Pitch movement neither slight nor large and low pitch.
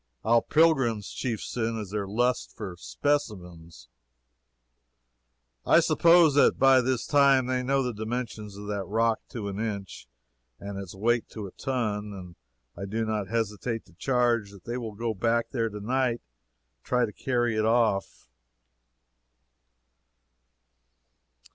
Yes: average, 3.5 semitones; low, 115 Hz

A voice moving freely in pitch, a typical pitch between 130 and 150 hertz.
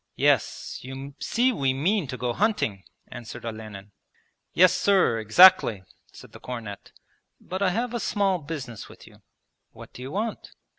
Yes: wide, 8.9 semitones; medium, 140 Hz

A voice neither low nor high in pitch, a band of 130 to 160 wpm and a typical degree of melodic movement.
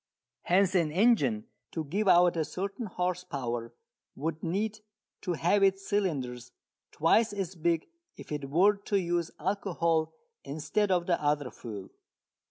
Yes: medium, 175 Hz; average, 145 wpm; average, 4.5 semitones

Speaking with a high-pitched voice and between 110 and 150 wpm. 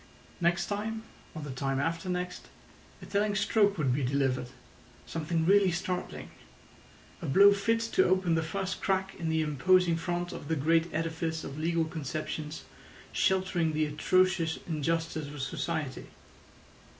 No: medium, 165 Hz; average, 140 wpm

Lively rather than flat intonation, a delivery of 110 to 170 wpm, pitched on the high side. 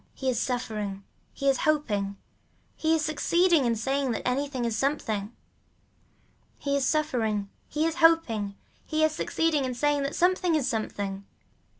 Yes: wide, 5.7 semitones; average, 155 wpm; very high, 275 Hz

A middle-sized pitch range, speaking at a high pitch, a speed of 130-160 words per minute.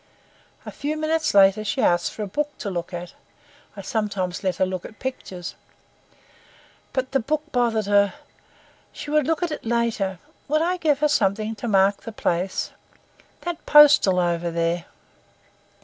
No: wide, 7.7 semitones; high, 215 Hz; average, 150 wpm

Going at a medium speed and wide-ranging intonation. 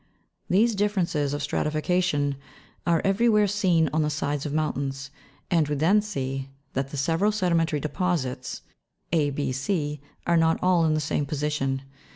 No: average, 155 wpm; average, 3.9 semitones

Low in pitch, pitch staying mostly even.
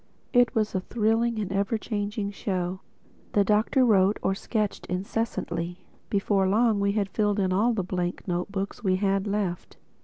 No: high, 200 Hz; narrow, 2.3 semitones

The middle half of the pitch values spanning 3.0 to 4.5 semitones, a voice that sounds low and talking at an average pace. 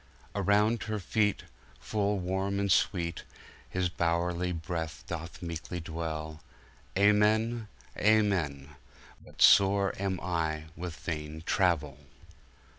No: average, 3.7 semitones; very low, 90 Hz; slow, 85 wpm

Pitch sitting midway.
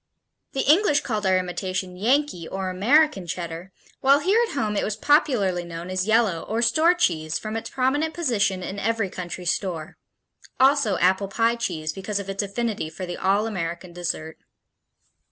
No: high, 200 Hz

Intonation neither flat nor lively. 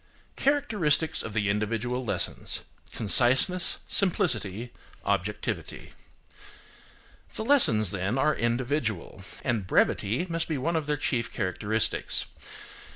No: wide, 7.2 semitones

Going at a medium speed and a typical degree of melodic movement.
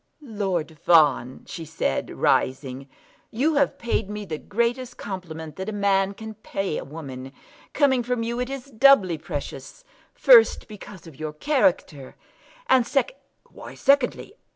No: average, 150 wpm; wide, 7.7 semitones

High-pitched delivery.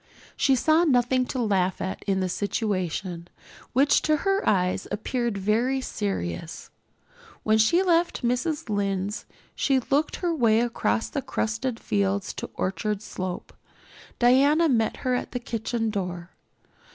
Yes: high, 225 Hz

